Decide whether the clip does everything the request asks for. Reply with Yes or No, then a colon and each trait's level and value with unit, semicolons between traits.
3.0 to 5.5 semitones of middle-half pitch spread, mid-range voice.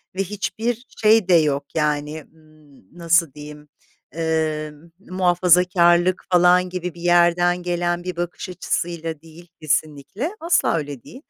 No: narrow, 2.6 semitones; medium, 175 Hz